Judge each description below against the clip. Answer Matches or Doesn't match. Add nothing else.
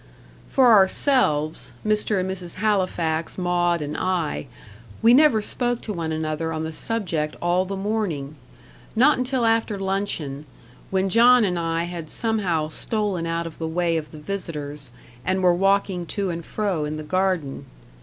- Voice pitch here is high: Doesn't match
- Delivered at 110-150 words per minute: Doesn't match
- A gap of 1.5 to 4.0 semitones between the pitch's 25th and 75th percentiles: Doesn't match